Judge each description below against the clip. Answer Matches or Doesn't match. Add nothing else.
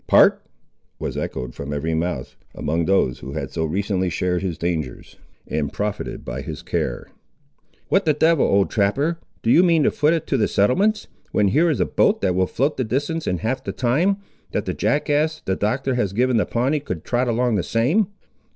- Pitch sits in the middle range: Doesn't match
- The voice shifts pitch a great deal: Matches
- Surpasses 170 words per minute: Matches